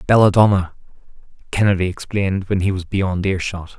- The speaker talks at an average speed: No, slow, 125 wpm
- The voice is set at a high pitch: No, very low, 95 Hz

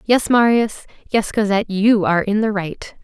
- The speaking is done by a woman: Yes, female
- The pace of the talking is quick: No, average, 180 wpm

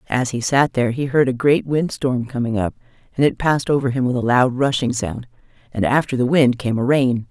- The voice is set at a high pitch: No, low, 130 Hz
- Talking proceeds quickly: Yes, fast, 240 wpm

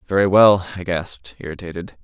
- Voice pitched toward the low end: Yes, very low, 90 Hz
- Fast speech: No, average, 150 wpm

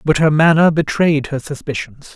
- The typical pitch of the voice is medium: Yes, medium, 150 Hz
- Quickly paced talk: No, average, 165 wpm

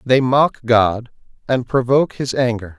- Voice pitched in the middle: No, low, 120 Hz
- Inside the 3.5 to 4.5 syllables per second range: Yes, 4.4 syllables/s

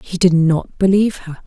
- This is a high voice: No, medium, 180 Hz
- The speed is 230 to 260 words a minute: No, fast, 205 wpm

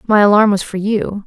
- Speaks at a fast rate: Yes, fast, 240 wpm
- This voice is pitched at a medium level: No, high, 205 Hz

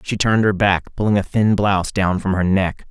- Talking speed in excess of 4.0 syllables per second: Yes, 5.4 syllables/s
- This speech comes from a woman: No, male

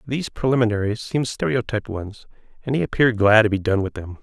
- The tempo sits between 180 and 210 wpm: Yes, average, 200 wpm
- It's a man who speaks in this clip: Yes, male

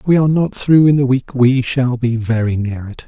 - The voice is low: Yes, low, 130 Hz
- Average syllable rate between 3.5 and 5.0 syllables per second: No, 5.3 syllables/s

